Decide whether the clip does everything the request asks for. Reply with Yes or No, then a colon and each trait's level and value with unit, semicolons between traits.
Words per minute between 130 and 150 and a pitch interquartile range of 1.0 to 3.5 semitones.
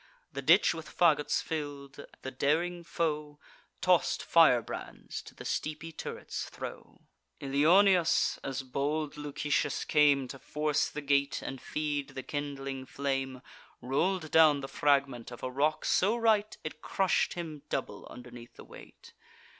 Yes: average, 140 wpm; narrow, 2.5 semitones